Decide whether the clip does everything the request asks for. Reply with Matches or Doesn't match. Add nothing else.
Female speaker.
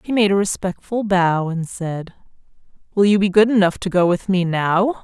Matches